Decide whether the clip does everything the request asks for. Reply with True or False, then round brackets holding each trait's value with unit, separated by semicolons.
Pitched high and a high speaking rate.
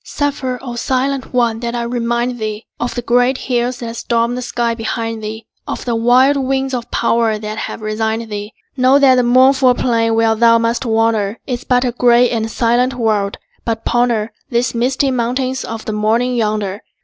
False (235 Hz; 185 wpm)